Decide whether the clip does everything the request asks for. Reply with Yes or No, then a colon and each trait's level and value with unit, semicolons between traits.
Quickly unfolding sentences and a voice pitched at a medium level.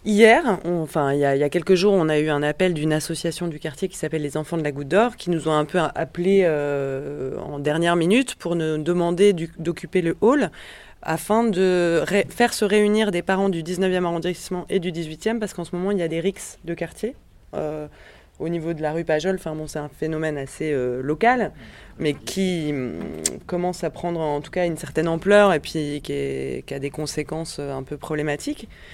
Yes: fast, 225 wpm; medium, 165 Hz